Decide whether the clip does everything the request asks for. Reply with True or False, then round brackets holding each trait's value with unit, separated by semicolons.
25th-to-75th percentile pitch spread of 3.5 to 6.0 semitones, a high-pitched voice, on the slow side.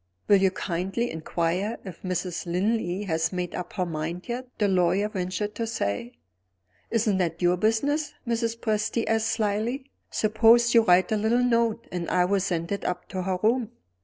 False (4.1 semitones; 200 Hz; 175 wpm)